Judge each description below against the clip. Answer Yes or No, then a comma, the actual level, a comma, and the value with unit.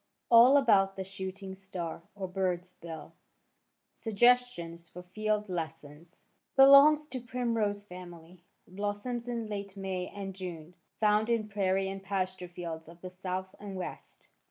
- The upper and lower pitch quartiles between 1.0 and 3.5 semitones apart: Yes, average, 3.0 semitones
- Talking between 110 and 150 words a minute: Yes, slow, 135 wpm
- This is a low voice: No, high, 195 Hz